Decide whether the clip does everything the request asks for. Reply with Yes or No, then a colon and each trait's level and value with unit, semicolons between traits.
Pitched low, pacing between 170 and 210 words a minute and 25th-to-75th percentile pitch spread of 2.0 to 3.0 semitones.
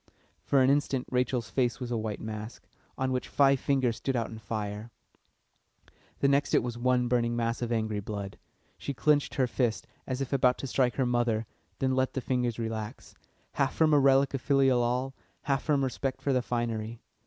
Yes: low, 125 Hz; average, 195 wpm; average, 2.7 semitones